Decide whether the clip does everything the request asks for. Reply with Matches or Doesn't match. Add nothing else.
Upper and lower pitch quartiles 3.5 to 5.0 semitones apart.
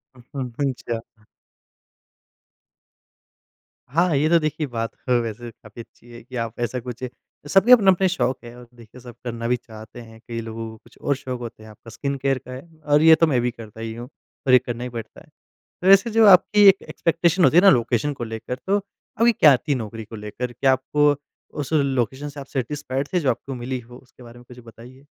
Matches